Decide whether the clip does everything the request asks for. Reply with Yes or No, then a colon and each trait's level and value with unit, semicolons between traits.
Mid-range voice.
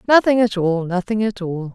No: high, 200 Hz